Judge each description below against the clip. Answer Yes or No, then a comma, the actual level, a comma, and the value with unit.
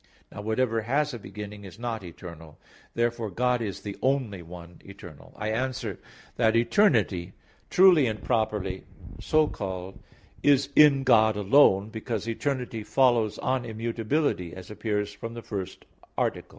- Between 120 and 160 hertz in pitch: No, low, 110 Hz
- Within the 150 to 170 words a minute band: No, average, 140 wpm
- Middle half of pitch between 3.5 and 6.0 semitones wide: Yes, average, 3.9 semitones